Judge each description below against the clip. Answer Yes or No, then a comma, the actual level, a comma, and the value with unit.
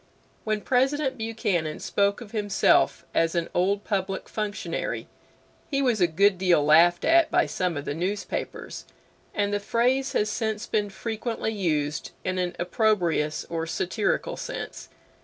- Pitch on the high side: Yes, high, 200 Hz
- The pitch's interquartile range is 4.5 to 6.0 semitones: No, average, 4.1 semitones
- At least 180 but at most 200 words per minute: No, average, 145 wpm